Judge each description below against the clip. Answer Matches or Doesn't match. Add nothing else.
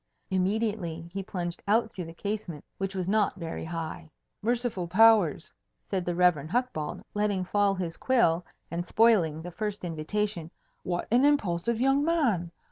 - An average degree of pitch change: Matches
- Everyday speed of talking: Matches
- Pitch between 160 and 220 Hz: Matches